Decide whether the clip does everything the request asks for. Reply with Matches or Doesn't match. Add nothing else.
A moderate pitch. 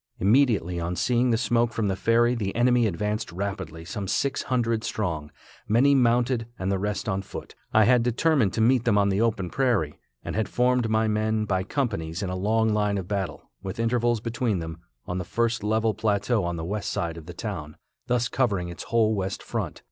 Doesn't match